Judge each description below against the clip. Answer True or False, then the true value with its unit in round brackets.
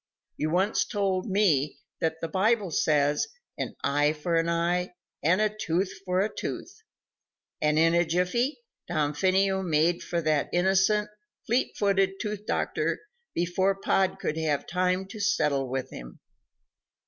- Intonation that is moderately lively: True (3.7 semitones)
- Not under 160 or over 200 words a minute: False (145 wpm)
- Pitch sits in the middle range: True (180 Hz)